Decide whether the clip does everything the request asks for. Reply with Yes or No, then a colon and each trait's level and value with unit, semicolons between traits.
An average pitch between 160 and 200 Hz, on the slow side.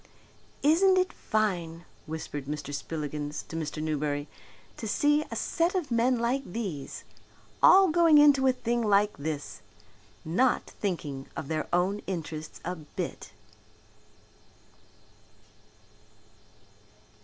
Yes: medium, 185 Hz; slow, 110 wpm